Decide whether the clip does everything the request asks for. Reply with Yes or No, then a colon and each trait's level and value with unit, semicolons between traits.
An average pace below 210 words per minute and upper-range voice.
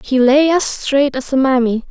No: fast, 220 wpm; very high, 270 Hz